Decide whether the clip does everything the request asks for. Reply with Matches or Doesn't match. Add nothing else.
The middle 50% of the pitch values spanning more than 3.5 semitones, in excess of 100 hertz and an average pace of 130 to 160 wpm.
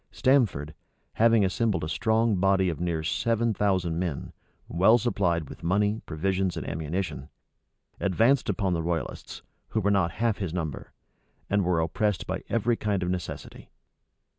Doesn't match